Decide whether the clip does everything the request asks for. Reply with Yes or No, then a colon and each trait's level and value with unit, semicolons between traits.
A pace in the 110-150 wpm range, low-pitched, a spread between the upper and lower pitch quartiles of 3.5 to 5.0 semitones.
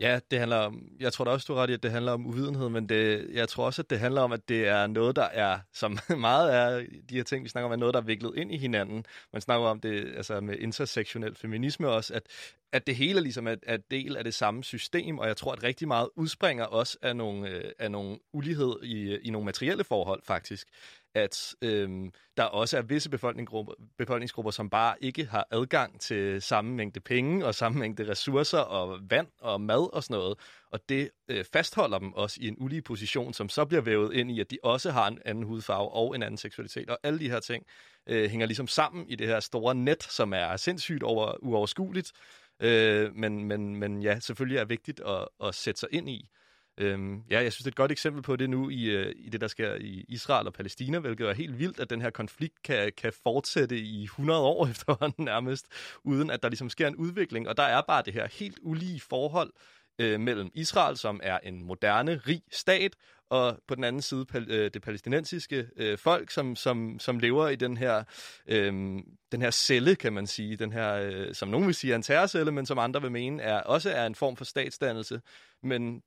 No: fast, 225 wpm; low, 120 Hz; average, 4.1 semitones